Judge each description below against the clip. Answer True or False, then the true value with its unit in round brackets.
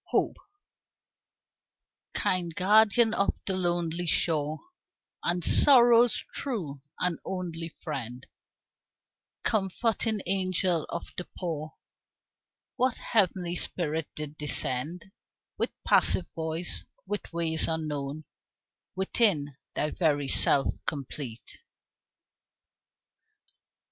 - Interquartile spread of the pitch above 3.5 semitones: True (4.0 semitones)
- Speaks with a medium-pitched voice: True (170 Hz)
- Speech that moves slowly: True (85 wpm)